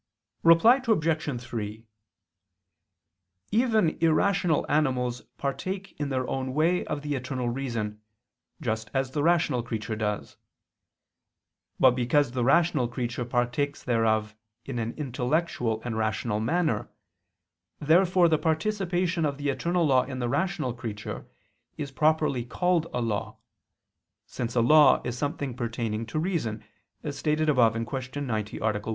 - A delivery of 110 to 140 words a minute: Yes, slow, 135 wpm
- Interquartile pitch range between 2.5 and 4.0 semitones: No, average, 5.1 semitones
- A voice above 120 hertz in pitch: Yes, low, 135 Hz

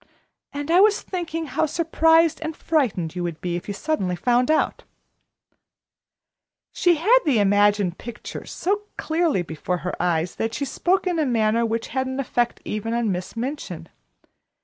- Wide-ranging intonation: Yes, wide, 8.1 semitones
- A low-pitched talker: No, high, 245 Hz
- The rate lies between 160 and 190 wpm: Yes, average, 170 wpm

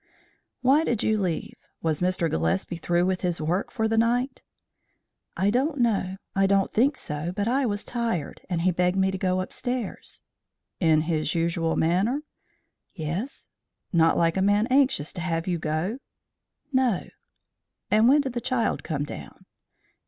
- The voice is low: No, high, 190 Hz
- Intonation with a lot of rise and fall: Yes, wide, 5.9 semitones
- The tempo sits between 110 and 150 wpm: No, average, 160 wpm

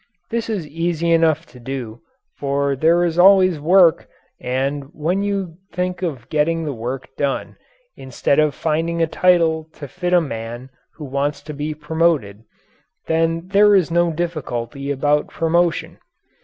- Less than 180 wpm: Yes, average, 150 wpm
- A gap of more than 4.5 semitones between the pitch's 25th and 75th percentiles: No, average, 3.7 semitones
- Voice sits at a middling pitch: Yes, medium, 160 Hz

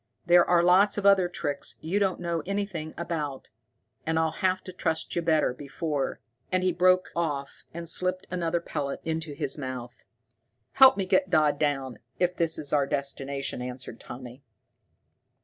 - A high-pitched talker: No, medium, 160 Hz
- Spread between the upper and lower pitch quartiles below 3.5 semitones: No, average, 4.5 semitones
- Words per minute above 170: No, average, 165 wpm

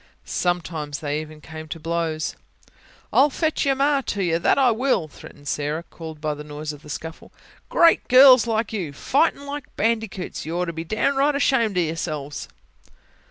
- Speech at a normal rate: Yes, average, 175 wpm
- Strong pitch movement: Yes, wide, 8.6 semitones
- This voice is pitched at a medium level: Yes, medium, 170 Hz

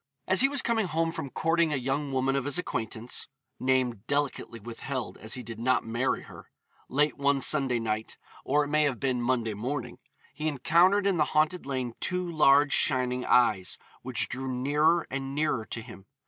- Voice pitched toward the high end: No, low, 135 Hz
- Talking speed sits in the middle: Yes, average, 185 wpm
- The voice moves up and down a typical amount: Yes, average, 3.6 semitones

